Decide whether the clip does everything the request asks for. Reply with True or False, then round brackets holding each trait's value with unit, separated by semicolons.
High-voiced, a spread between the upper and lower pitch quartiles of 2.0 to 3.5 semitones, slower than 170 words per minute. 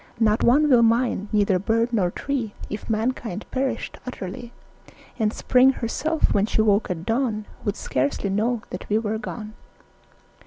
True (220 Hz; 2.8 semitones; 155 wpm)